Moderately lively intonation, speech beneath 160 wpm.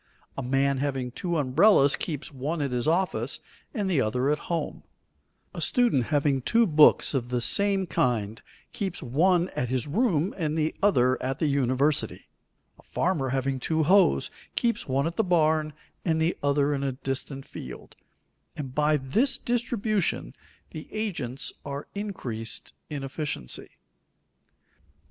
Yes: average, 5.0 semitones; average, 150 wpm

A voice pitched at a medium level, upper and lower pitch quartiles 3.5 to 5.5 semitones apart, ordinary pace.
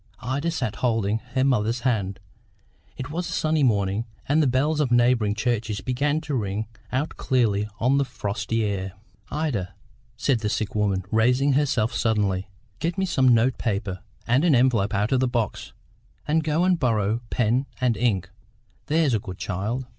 No: low, 120 Hz; average, 4.7 semitones; average, 170 wpm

